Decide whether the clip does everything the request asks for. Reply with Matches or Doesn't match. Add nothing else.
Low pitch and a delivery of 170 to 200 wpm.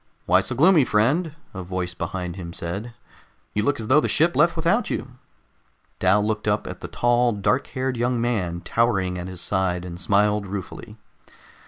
Matches